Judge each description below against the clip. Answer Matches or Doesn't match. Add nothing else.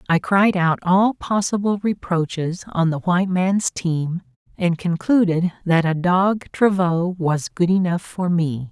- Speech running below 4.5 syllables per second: Matches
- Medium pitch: Matches